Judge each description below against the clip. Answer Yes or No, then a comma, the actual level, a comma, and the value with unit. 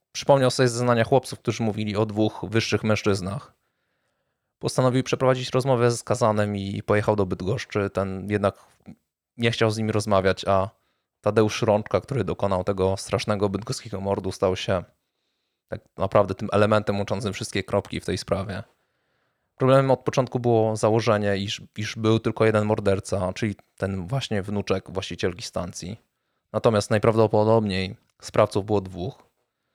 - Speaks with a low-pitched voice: Yes, low, 105 Hz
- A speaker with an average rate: Yes, average, 140 wpm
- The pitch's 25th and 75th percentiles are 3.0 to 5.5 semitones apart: No, narrow, 2.6 semitones